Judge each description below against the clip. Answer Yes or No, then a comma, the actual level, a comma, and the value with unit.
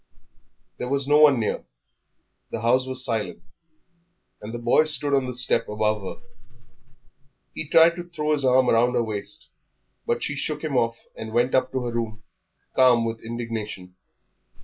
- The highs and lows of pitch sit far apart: No, average, 3.5 semitones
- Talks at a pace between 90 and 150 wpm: No, average, 170 wpm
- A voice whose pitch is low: Yes, low, 125 Hz